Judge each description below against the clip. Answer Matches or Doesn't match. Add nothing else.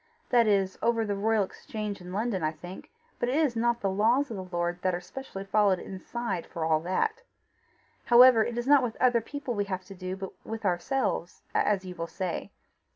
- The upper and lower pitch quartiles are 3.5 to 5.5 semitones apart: Matches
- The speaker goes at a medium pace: Doesn't match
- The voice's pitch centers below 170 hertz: Doesn't match